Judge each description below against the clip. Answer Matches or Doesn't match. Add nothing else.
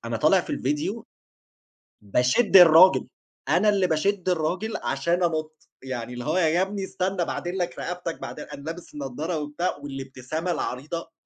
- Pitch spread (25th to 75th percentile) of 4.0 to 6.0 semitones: Matches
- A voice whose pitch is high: Doesn't match